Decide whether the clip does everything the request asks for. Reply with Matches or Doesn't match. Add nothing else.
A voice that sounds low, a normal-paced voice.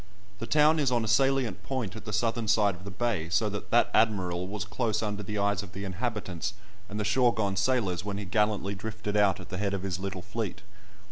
Doesn't match